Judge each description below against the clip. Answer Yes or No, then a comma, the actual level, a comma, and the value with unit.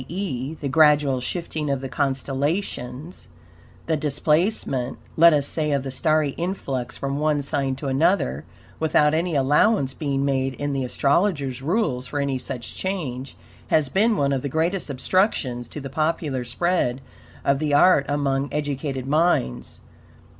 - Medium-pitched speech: Yes, medium, 145 Hz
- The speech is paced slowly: No, average, 150 wpm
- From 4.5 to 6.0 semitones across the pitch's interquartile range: No, average, 3.1 semitones